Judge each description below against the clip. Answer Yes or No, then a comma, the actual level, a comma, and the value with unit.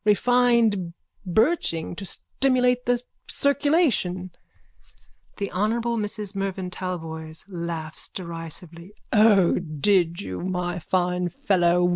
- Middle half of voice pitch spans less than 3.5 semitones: No, average, 4.6 semitones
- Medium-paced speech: No, slow, 95 wpm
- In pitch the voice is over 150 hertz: Yes, medium, 185 Hz